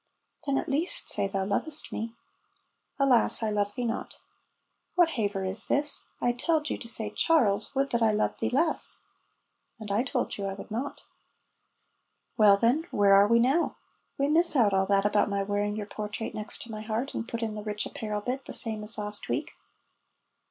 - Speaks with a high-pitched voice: Yes, high, 220 Hz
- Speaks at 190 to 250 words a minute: Yes, average, 195 wpm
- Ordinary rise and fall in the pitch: Yes, average, 4.4 semitones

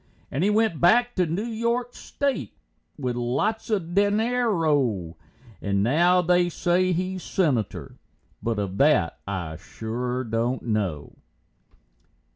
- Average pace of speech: No, slow, 120 wpm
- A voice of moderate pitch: Yes, medium, 165 Hz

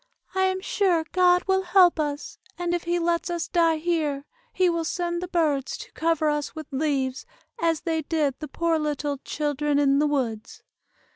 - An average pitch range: Yes, average, 3.0 semitones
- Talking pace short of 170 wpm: No, average, 185 wpm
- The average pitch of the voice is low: No, very high, 320 Hz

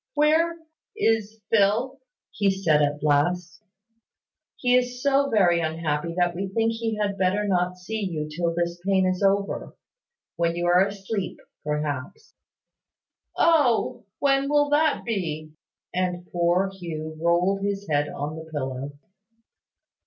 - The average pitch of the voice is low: No, medium, 185 Hz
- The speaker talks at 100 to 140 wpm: Yes, slow, 135 wpm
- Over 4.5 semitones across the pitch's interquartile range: Yes, average, 4.9 semitones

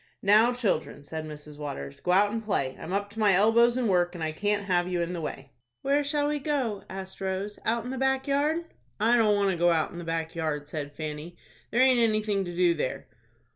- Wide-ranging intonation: Yes, wide, 5.9 semitones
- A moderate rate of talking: No, fast, 235 wpm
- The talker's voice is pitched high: Yes, high, 195 Hz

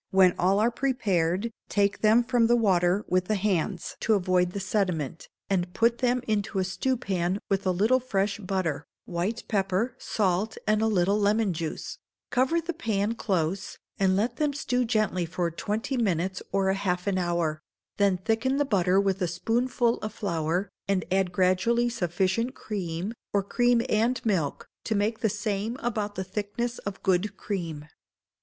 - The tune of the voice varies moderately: Yes, average, 3.8 semitones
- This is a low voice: No, high, 200 Hz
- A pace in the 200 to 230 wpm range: No, average, 165 wpm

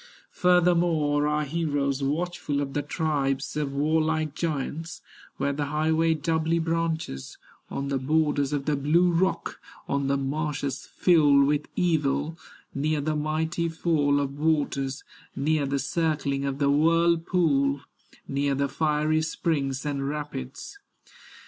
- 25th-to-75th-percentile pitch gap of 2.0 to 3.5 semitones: Yes, narrow, 2.4 semitones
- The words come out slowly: Yes, slow, 130 wpm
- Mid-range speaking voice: Yes, medium, 150 Hz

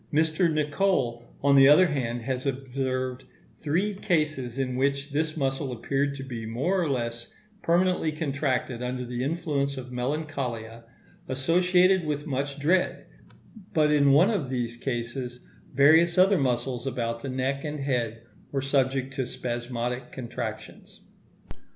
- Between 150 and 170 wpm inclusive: No, average, 140 wpm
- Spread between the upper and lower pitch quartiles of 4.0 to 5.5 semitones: No, average, 3.5 semitones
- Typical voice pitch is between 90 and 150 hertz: Yes, low, 135 Hz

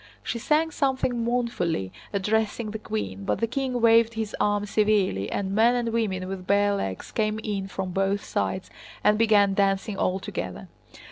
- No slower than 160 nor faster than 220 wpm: Yes, average, 165 wpm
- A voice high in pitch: Yes, high, 210 Hz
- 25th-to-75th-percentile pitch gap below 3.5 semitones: Yes, average, 3.0 semitones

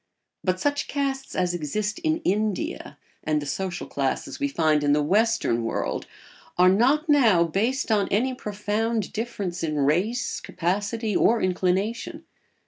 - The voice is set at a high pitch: Yes, high, 205 Hz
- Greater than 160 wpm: No, average, 140 wpm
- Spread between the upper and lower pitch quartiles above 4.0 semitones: Yes, average, 5.0 semitones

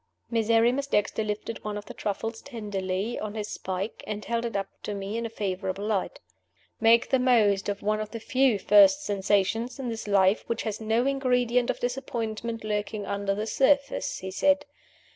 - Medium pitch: No, high, 220 Hz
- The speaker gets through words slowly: No, average, 180 wpm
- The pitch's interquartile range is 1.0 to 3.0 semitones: Yes, average, 2.7 semitones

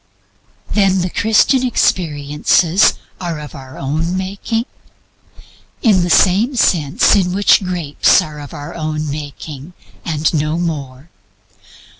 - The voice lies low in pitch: No, medium, 165 Hz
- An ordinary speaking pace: No, slow, 110 wpm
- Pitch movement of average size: Yes, average, 4.1 semitones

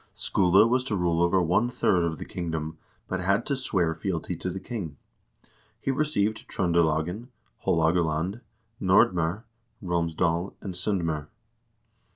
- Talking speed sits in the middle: No, slow, 130 wpm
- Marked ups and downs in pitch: No, average, 3.4 semitones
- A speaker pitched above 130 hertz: No, very low, 90 Hz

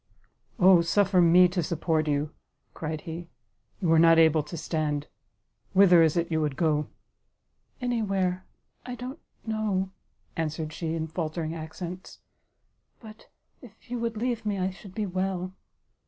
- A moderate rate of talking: Yes, average, 155 wpm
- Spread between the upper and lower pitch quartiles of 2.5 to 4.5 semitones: Yes, average, 3.7 semitones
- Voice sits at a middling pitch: Yes, medium, 175 Hz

